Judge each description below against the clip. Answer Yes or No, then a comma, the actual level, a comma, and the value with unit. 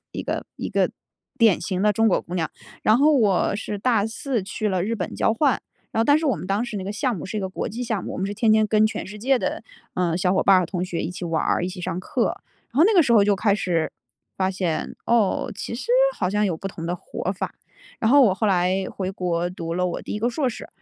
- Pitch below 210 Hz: Yes, high, 200 Hz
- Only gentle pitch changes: No, average, 3.6 semitones